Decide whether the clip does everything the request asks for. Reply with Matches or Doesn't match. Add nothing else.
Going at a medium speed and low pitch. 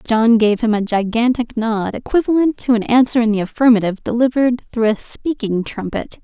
Doesn't match